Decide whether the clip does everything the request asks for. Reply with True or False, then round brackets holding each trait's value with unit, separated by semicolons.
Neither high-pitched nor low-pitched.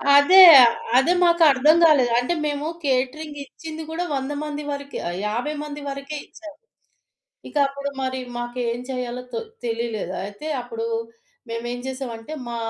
False (270 Hz)